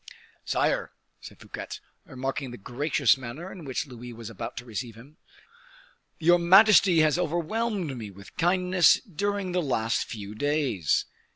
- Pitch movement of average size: No, wide, 6.8 semitones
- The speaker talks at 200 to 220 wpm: No, average, 145 wpm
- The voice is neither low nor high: Yes, medium, 145 Hz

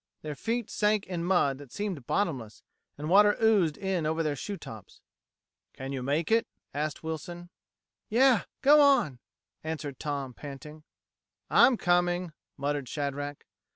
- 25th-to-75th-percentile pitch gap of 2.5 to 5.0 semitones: No, wide, 5.6 semitones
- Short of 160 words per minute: Yes, average, 140 wpm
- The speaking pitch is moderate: Yes, medium, 160 Hz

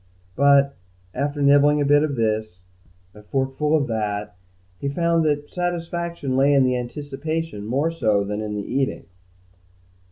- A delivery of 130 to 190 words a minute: Yes, average, 150 wpm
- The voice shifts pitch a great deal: No, average, 4.8 semitones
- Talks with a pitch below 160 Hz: Yes, medium, 140 Hz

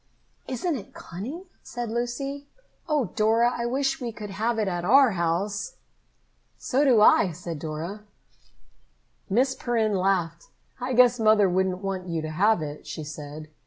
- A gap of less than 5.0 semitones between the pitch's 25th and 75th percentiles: No, wide, 5.5 semitones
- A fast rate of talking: No, average, 155 wpm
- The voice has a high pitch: Yes, high, 215 Hz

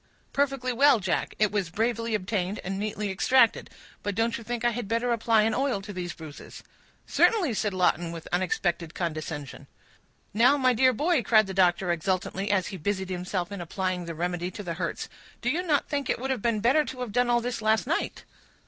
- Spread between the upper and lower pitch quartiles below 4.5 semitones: No, average, 5.0 semitones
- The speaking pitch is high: Yes, high, 210 Hz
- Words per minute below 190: No, fast, 205 wpm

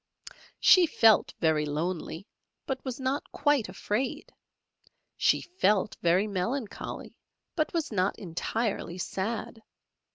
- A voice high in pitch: Yes, high, 210 Hz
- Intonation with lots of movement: Yes, wide, 6.3 semitones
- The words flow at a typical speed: No, slow, 105 wpm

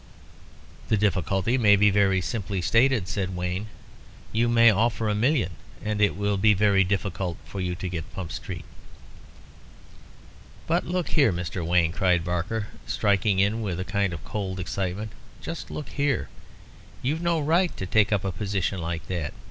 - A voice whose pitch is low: Yes, low, 100 Hz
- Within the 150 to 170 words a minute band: Yes, average, 165 wpm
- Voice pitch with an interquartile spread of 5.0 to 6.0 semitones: No, average, 3.3 semitones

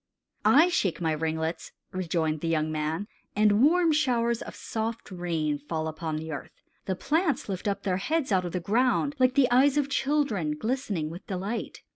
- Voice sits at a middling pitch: No, high, 195 Hz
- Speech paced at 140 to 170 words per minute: No, average, 180 wpm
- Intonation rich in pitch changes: Yes, wide, 7.9 semitones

